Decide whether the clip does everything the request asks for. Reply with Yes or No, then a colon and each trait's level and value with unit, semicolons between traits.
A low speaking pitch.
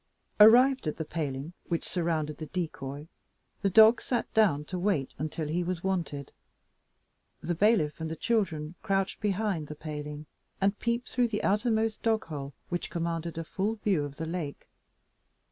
No: medium, 170 Hz